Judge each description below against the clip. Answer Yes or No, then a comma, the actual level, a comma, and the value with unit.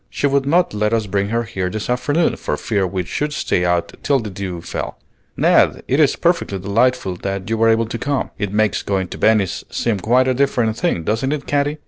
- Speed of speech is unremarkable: No, fast, 220 wpm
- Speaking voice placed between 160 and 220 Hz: No, low, 110 Hz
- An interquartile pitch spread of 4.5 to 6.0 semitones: Yes, average, 4.8 semitones